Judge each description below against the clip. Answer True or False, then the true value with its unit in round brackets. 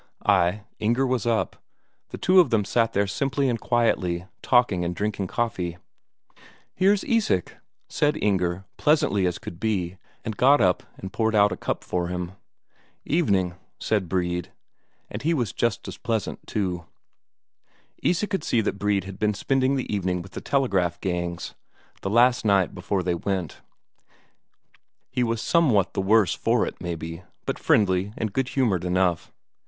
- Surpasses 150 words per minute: True (160 wpm)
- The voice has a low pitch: True (100 Hz)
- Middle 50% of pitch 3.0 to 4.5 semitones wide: False (5.0 semitones)